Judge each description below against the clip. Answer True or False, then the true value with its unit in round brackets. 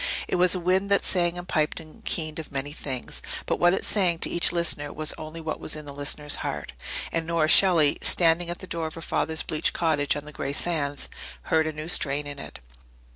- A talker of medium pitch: True (160 Hz)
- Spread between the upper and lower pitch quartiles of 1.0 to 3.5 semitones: True (2.7 semitones)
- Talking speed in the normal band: False (230 wpm)